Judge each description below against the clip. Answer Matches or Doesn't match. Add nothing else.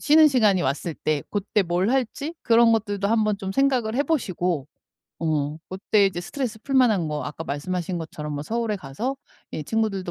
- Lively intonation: Matches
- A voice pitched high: Matches